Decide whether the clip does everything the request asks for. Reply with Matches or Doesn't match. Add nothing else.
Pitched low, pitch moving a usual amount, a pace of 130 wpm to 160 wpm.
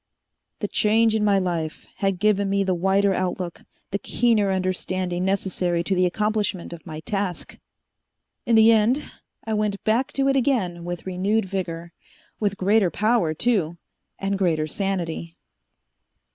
Doesn't match